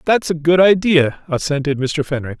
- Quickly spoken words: No, average, 175 wpm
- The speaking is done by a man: Yes, male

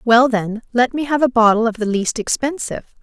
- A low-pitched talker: No, high, 240 Hz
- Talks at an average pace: No, fast, 220 wpm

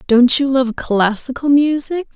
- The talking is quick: No, average, 140 wpm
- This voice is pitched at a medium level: No, very high, 265 Hz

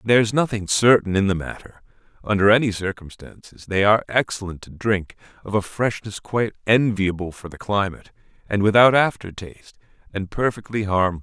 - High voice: No, low, 105 Hz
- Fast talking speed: No, average, 160 wpm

